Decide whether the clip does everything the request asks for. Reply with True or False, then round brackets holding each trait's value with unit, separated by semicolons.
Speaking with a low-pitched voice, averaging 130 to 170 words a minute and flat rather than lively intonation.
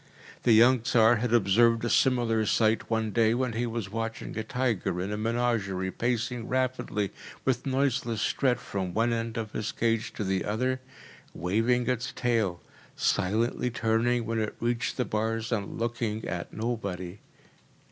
True (115 Hz; 155 wpm; 2.0 semitones)